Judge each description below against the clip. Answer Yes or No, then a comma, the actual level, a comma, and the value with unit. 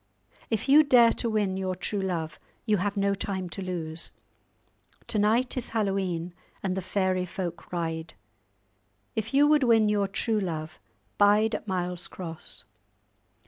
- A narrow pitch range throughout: No, average, 3.4 semitones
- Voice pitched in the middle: No, high, 195 Hz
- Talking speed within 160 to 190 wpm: No, average, 150 wpm